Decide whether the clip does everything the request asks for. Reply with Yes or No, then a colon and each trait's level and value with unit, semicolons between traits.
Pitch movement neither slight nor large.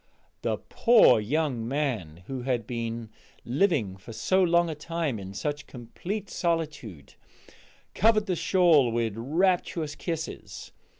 No: wide, 6.8 semitones